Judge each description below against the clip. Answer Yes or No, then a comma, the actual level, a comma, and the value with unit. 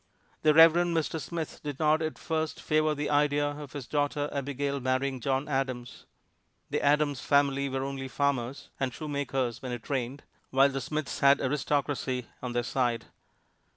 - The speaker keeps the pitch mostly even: Yes, narrow, 2.1 semitones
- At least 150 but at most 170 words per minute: Yes, average, 160 wpm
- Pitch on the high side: No, medium, 140 Hz